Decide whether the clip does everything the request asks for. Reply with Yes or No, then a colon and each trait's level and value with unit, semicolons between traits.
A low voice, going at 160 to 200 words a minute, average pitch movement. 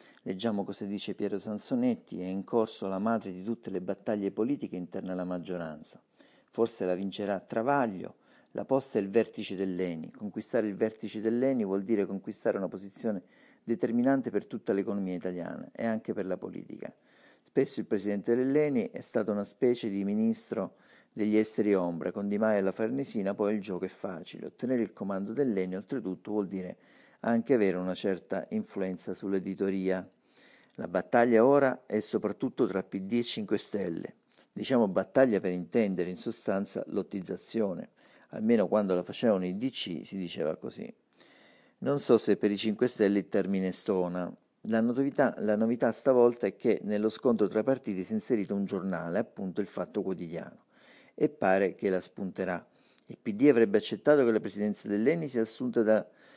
Yes: low, 105 Hz; average, 165 wpm; average, 3.2 semitones